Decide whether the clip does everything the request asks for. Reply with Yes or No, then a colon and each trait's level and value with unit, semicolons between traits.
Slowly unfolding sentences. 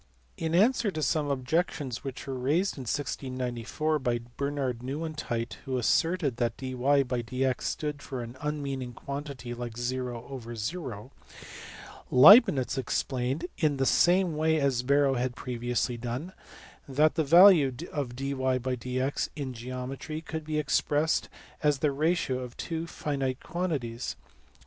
Yes: slow, 125 wpm